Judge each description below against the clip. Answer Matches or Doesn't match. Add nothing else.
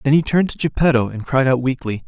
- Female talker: Doesn't match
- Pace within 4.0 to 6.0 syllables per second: Doesn't match